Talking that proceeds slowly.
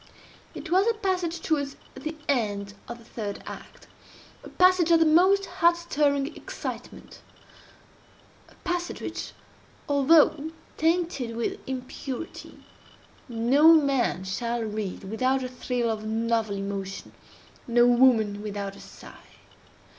Yes: slow, 115 wpm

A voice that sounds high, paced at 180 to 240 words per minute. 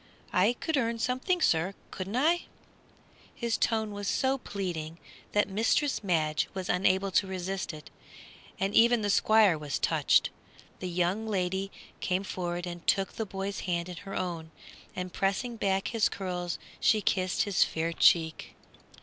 No: high, 195 Hz; average, 155 wpm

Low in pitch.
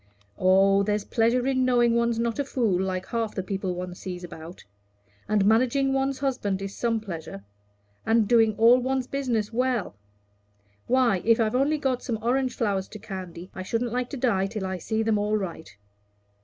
No: high, 225 Hz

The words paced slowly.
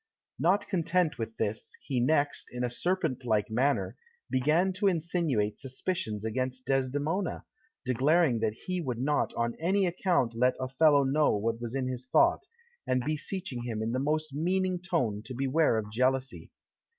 No: average, 160 wpm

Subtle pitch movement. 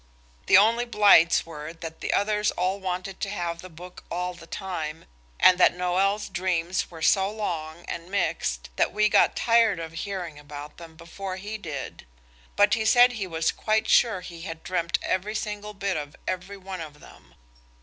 No: average, 3.5 semitones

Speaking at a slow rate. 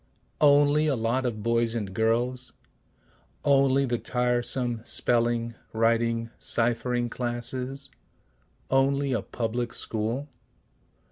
Yes: slow, 95 wpm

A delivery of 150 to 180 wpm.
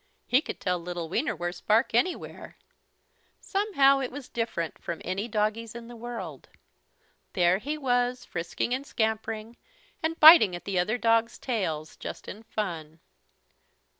No: average, 140 wpm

